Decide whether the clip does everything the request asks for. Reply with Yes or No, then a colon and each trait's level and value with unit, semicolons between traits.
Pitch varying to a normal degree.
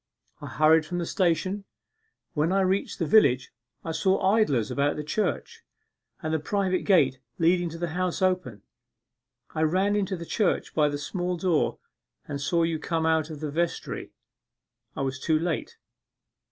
Yes: average, 3.4 semitones